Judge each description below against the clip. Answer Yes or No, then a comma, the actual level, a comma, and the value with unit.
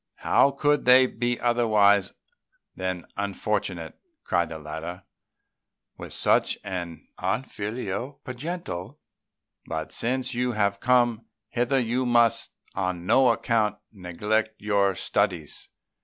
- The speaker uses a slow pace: Yes, slow, 110 wpm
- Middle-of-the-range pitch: No, low, 110 Hz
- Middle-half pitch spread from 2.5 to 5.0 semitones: Yes, average, 4.7 semitones